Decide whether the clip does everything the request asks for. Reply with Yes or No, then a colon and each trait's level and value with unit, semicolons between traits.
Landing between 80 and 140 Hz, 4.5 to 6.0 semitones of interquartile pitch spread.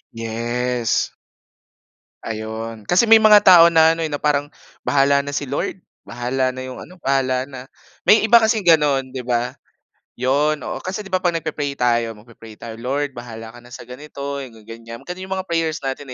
Yes: low, 135 Hz; average, 5.3 semitones